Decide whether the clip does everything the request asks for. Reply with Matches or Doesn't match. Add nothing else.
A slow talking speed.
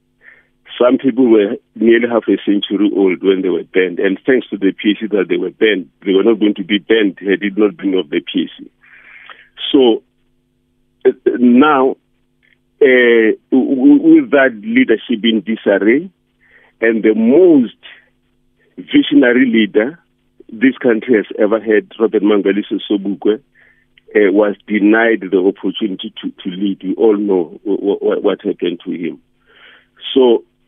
Doesn't match